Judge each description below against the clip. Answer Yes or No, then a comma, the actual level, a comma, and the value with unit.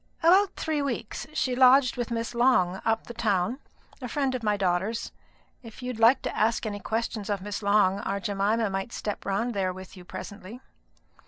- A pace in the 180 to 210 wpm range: Yes, average, 185 wpm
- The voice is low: No, high, 225 Hz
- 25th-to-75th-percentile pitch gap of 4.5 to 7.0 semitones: No, average, 3.8 semitones